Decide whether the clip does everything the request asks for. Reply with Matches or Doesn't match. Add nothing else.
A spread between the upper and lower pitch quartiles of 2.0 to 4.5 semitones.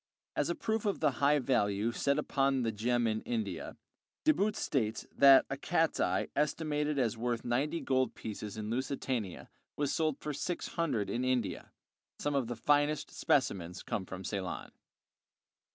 Doesn't match